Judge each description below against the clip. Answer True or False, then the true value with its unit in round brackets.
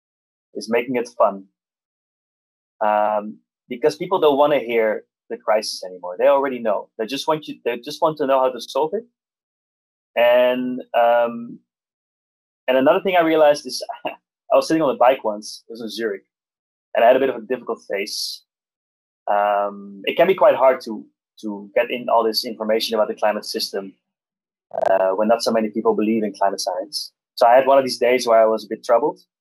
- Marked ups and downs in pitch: False (4.1 semitones)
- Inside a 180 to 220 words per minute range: True (200 wpm)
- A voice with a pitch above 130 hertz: False (115 Hz)